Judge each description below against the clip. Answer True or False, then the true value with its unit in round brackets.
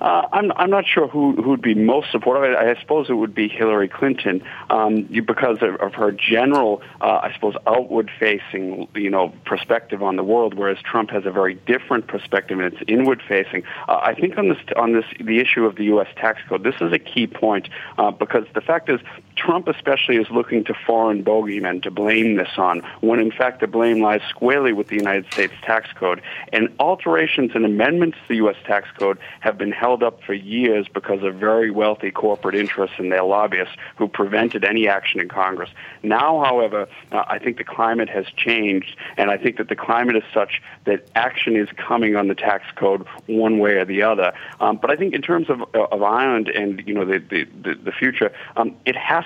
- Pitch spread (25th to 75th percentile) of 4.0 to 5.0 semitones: False (2.6 semitones)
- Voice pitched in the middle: False (110 Hz)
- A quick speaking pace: True (210 wpm)